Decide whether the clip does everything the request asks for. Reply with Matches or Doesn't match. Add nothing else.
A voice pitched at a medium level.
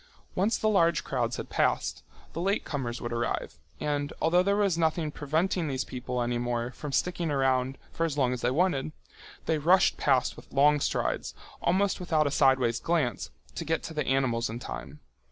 Matches